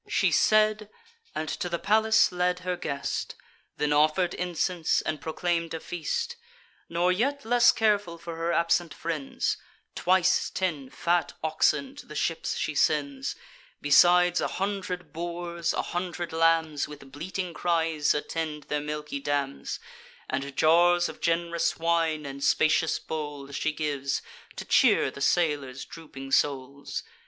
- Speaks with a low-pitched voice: No, medium, 165 Hz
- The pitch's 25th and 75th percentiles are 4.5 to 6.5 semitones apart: No, average, 3.2 semitones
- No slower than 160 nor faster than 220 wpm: No, average, 140 wpm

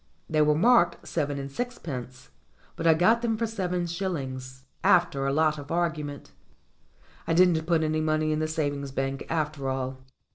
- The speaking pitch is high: No, medium, 155 Hz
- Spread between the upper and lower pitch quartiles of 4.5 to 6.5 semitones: No, average, 3.7 semitones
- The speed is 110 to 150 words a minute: No, average, 170 wpm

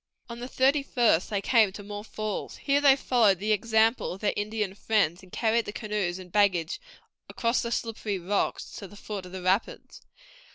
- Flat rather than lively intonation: No, average, 3.1 semitones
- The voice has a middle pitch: No, high, 210 Hz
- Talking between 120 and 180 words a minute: No, average, 195 wpm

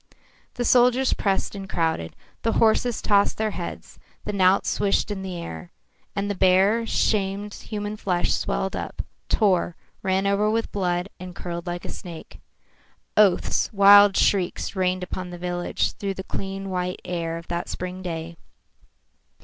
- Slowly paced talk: No, average, 155 wpm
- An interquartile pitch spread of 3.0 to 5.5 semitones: No, narrow, 2.4 semitones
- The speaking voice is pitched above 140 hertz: Yes, high, 190 Hz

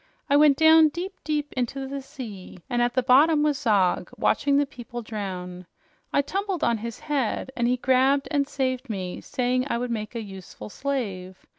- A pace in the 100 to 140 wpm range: No, average, 185 wpm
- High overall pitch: Yes, very high, 255 Hz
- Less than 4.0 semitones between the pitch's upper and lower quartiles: No, average, 4.5 semitones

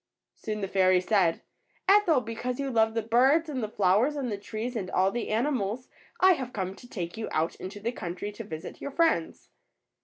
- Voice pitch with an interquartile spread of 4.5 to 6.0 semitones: Yes, average, 4.9 semitones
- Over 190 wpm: Yes, fast, 205 wpm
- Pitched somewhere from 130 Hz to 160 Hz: No, high, 225 Hz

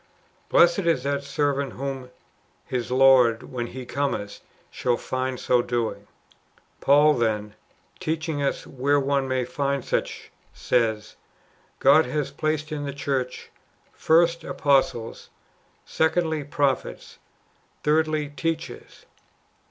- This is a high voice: No, medium, 140 Hz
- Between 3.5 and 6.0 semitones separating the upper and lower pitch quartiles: No, average, 3.1 semitones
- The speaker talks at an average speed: No, slow, 115 wpm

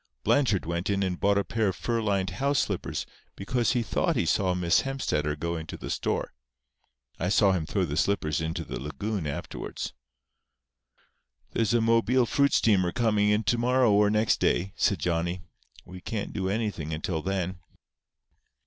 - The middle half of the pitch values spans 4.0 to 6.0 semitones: Yes, average, 4.5 semitones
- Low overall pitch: Yes, low, 100 Hz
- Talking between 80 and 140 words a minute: No, average, 170 wpm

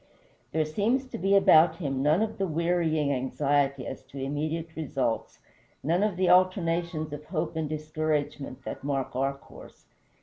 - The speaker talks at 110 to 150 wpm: No, average, 160 wpm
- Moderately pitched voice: Yes, medium, 155 Hz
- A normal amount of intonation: Yes, average, 3.5 semitones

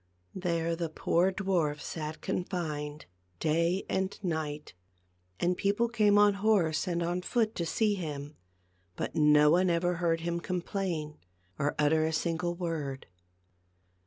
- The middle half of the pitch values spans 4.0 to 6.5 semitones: No, average, 3.2 semitones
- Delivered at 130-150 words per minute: Yes, average, 140 wpm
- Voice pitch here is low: No, medium, 170 Hz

